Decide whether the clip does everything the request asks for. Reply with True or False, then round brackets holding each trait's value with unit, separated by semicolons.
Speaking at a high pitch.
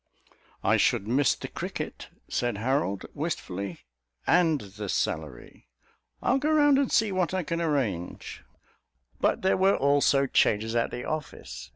False (140 Hz)